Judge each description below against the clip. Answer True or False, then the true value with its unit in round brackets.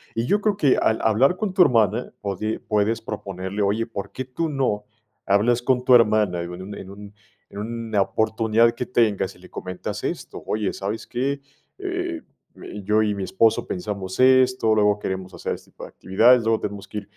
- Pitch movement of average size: True (3.7 semitones)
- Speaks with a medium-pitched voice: False (110 Hz)